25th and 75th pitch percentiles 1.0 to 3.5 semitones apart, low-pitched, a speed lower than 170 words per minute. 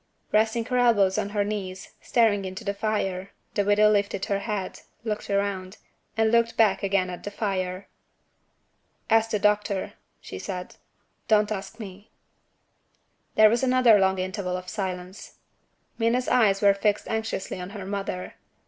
No: narrow, 2.4 semitones; high, 205 Hz; average, 150 wpm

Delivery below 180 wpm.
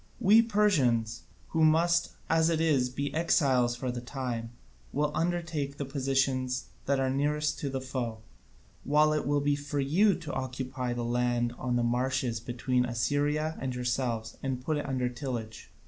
Yes: average, 165 wpm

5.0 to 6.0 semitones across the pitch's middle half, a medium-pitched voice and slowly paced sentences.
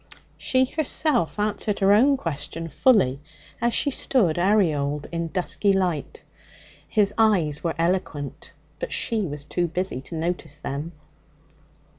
Yes: wide, 5.4 semitones; medium, 180 Hz; slow, 130 wpm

